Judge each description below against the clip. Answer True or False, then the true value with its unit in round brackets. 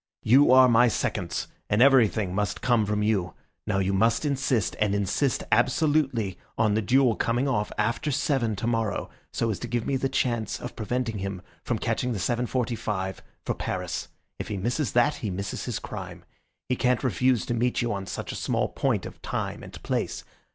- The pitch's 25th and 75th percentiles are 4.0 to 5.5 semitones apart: False (3.5 semitones)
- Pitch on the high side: False (115 Hz)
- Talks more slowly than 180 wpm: False (185 wpm)